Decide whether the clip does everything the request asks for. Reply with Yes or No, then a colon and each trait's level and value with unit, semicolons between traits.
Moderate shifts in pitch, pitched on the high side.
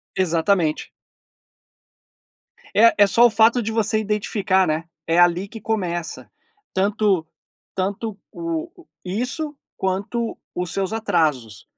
Yes: average, 4.2 semitones; high, 200 Hz